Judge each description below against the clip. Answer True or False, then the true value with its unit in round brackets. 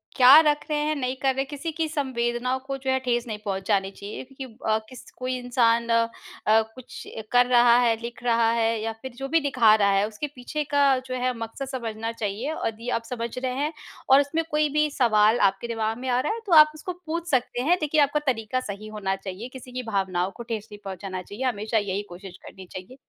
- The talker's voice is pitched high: True (240 Hz)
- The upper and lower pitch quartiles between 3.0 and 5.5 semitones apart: True (3.7 semitones)